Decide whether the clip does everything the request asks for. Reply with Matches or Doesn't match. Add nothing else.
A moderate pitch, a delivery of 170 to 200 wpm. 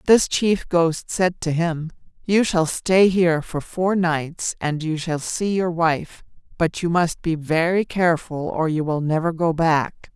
Matches